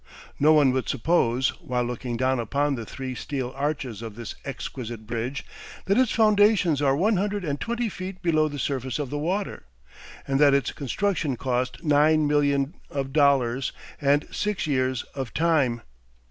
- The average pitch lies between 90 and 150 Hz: Yes, medium, 140 Hz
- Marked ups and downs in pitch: No, average, 3.6 semitones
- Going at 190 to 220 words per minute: No, average, 165 wpm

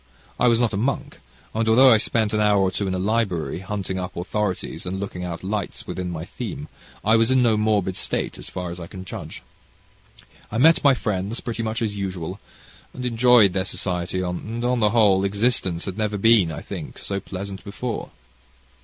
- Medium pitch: No, low, 100 Hz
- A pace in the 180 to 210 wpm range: Yes, average, 200 wpm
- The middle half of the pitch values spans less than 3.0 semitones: No, average, 3.4 semitones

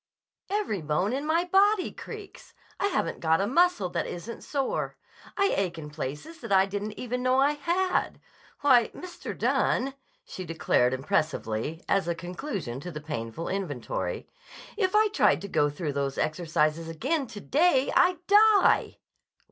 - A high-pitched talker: Yes, high, 200 Hz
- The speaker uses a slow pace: No, average, 155 wpm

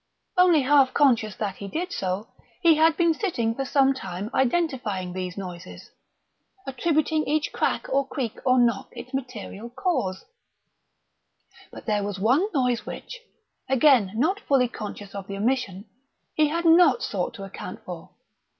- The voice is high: Yes, very high, 250 Hz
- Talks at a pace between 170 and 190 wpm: No, average, 155 wpm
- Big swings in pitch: Yes, wide, 7.0 semitones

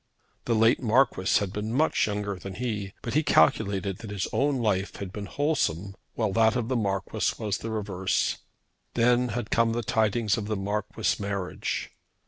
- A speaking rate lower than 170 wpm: No, average, 175 wpm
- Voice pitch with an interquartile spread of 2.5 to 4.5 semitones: Yes, average, 2.9 semitones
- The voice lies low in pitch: Yes, low, 105 Hz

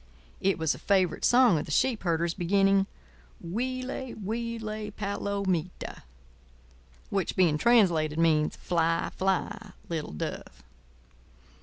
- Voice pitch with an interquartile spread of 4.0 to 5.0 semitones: Yes, average, 4.5 semitones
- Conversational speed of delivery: No, slow, 110 wpm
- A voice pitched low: No, high, 190 Hz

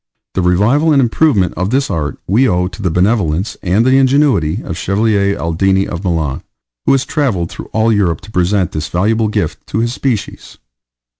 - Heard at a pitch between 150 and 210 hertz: No, low, 100 Hz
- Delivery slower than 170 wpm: No, average, 195 wpm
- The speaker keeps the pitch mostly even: No, average, 4.8 semitones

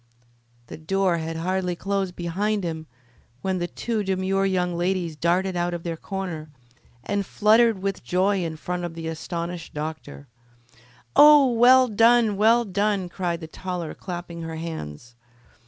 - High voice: No, medium, 180 Hz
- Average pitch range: Yes, average, 3.0 semitones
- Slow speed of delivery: No, average, 150 wpm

